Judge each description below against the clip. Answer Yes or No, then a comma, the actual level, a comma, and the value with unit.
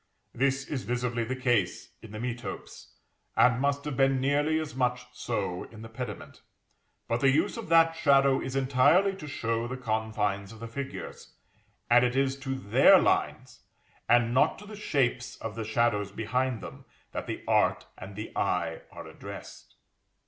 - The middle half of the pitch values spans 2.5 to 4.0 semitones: Yes, average, 3.3 semitones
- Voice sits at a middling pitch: No, low, 125 Hz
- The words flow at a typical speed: Yes, average, 170 wpm